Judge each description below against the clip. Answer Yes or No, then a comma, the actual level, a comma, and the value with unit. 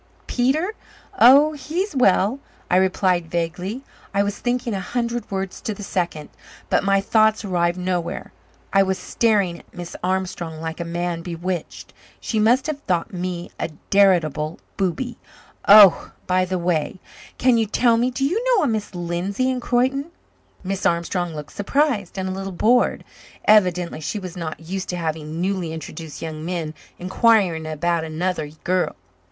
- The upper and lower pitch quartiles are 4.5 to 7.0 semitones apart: Yes, average, 4.8 semitones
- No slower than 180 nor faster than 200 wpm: No, average, 160 wpm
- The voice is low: No, medium, 185 Hz